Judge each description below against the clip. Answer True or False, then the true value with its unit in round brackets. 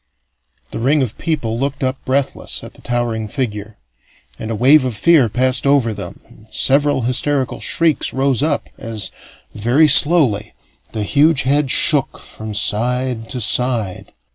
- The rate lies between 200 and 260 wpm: False (150 wpm)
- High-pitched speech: False (130 Hz)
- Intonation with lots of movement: False (4.0 semitones)